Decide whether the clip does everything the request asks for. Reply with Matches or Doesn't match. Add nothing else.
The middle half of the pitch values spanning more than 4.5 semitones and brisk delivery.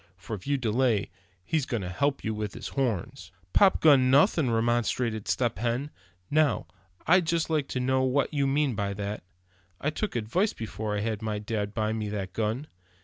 Doesn't match